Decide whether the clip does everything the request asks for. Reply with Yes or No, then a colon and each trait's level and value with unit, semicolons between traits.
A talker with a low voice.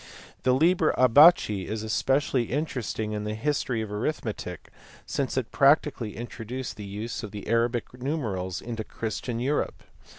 Yes: low, 120 Hz